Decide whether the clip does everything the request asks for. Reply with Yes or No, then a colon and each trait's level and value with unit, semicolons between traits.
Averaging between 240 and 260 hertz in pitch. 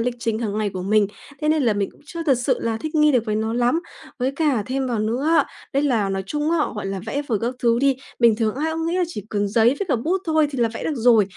Yes: high, 245 Hz